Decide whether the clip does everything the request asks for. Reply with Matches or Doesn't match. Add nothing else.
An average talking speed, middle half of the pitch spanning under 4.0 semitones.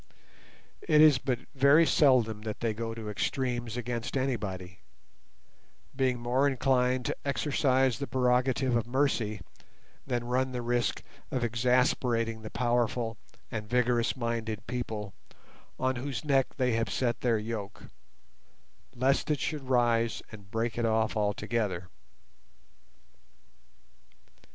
Doesn't match